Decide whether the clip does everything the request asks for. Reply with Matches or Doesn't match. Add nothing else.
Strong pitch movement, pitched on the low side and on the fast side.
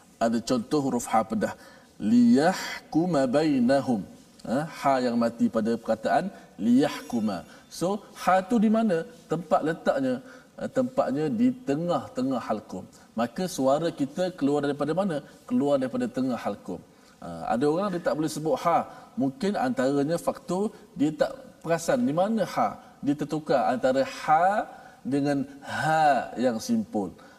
Doesn't match